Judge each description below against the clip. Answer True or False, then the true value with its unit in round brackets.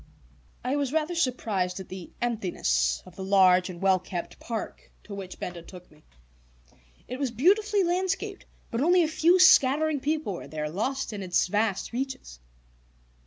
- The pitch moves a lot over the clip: True (9.0 semitones)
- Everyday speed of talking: True (165 wpm)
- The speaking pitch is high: True (225 Hz)